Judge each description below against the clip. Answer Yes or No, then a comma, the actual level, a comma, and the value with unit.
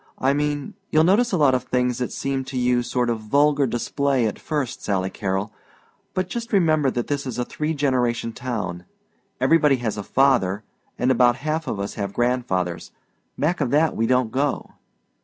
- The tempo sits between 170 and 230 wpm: Yes, average, 185 wpm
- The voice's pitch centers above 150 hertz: No, low, 130 Hz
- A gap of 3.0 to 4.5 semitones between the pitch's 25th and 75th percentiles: Yes, average, 3.9 semitones